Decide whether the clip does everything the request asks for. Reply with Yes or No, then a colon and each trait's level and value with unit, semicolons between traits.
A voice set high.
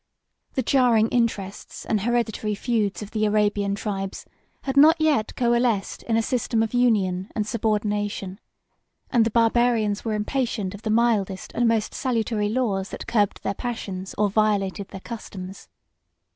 Yes: high, 215 Hz